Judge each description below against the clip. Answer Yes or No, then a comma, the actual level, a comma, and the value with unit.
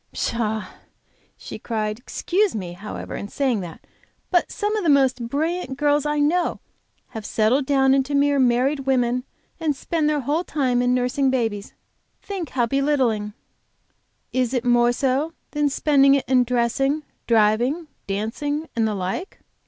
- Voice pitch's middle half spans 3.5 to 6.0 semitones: Yes, average, 3.9 semitones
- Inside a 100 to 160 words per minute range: Yes, average, 150 wpm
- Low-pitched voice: No, very high, 265 Hz